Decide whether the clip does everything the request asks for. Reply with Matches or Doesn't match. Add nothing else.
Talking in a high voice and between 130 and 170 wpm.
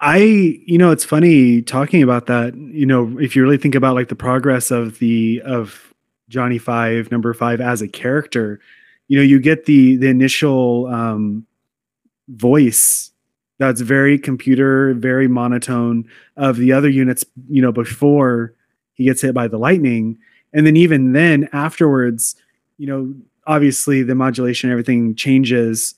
Doesn't match